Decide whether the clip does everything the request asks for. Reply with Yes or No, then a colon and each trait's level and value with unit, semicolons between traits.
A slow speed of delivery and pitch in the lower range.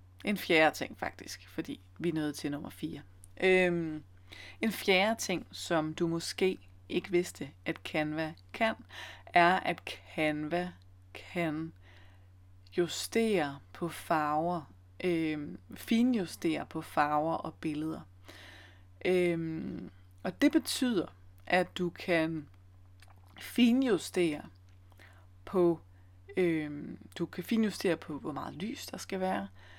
No: slow, 115 wpm; medium, 155 Hz